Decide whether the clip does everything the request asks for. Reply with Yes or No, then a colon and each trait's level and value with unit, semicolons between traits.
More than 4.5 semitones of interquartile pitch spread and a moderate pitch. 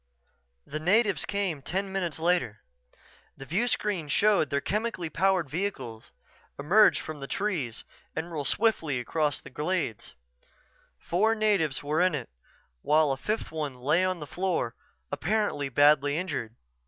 Yes: average, 5.2 semitones; medium, 160 Hz